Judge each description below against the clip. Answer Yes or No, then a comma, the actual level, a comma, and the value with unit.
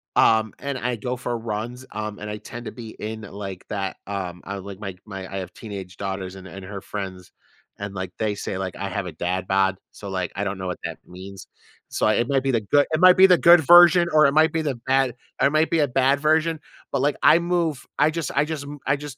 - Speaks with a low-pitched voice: Yes, low, 110 Hz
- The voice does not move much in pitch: No, wide, 6.8 semitones